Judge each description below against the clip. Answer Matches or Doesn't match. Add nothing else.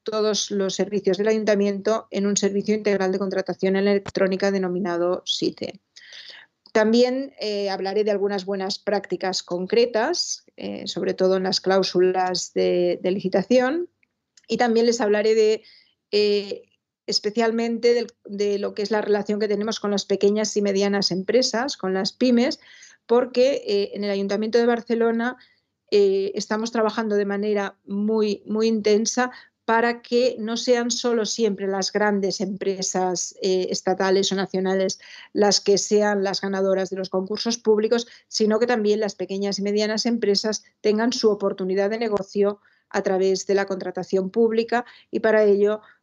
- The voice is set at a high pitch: Matches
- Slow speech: Doesn't match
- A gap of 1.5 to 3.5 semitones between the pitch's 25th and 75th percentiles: Matches